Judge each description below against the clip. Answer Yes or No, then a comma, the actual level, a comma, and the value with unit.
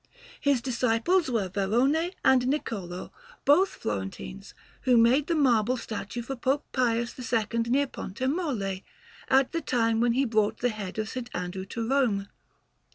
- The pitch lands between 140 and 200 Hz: No, high, 235 Hz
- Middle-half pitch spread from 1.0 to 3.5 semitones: No, average, 4.0 semitones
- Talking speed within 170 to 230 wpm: No, average, 150 wpm